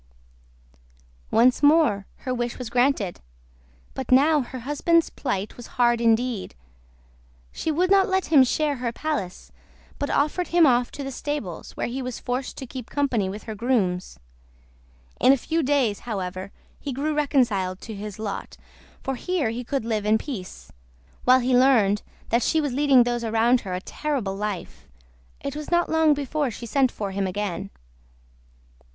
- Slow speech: No, average, 165 wpm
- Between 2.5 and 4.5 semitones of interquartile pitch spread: No, average, 5.1 semitones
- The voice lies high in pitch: Yes, very high, 250 Hz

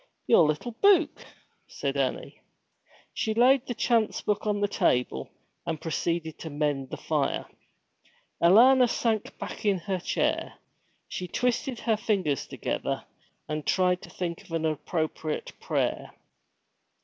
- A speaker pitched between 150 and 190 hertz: Yes, medium, 185 Hz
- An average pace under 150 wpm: Yes, slow, 135 wpm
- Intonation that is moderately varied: No, wide, 6.2 semitones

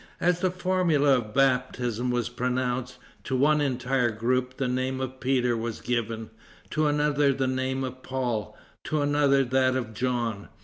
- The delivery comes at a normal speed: Yes, average, 160 wpm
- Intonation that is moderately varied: No, narrow, 2.1 semitones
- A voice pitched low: Yes, low, 130 Hz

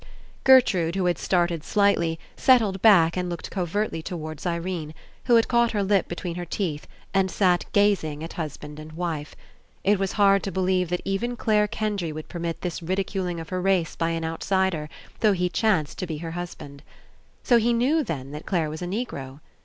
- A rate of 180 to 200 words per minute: Yes, average, 190 wpm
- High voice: No, medium, 180 Hz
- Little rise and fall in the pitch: No, average, 3.6 semitones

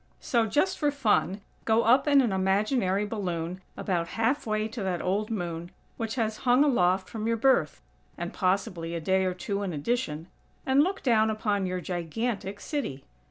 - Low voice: No, high, 210 Hz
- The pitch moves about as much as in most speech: Yes, average, 4.3 semitones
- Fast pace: No, average, 175 wpm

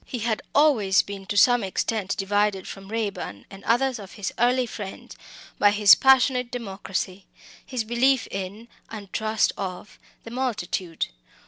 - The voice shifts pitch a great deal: No, average, 3.7 semitones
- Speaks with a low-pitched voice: No, high, 210 Hz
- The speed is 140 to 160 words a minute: Yes, average, 145 wpm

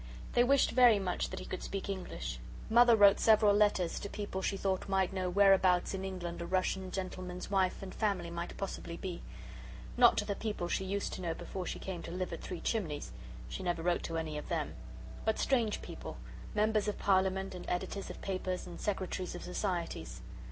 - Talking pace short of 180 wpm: No, average, 200 wpm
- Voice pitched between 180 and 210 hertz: Yes, high, 190 Hz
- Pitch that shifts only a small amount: Yes, narrow, 2.2 semitones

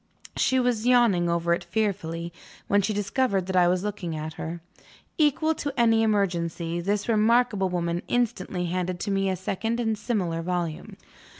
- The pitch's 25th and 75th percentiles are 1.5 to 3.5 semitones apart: No, average, 4.6 semitones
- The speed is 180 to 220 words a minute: No, average, 165 wpm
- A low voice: No, high, 195 Hz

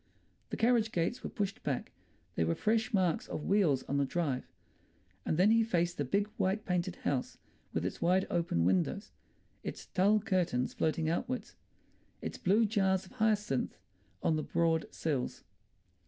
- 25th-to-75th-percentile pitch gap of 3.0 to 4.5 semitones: No, average, 5.3 semitones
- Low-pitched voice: No, medium, 180 Hz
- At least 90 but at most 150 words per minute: No, average, 160 wpm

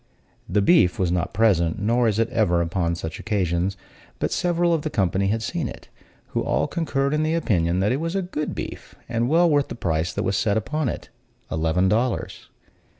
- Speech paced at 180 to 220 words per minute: Yes, fast, 205 wpm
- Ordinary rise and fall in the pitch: No, wide, 8.4 semitones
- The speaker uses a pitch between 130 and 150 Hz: No, low, 110 Hz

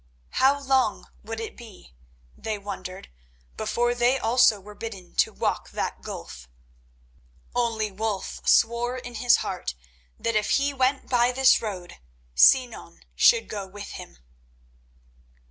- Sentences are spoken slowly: Yes, slow, 130 wpm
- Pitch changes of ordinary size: Yes, average, 3.5 semitones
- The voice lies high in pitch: Yes, high, 225 Hz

